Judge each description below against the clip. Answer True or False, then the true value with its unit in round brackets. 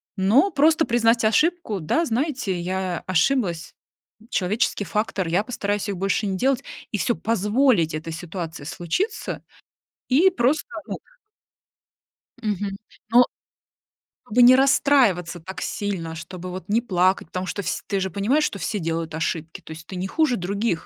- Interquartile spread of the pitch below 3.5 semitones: False (5.5 semitones)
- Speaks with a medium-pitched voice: False (200 Hz)